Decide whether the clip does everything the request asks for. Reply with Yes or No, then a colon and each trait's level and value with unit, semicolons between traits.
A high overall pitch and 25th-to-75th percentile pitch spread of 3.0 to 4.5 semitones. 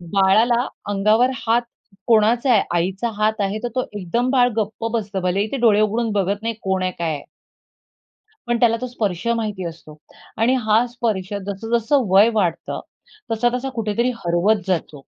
Yes: high, 215 Hz; average, 3.5 semitones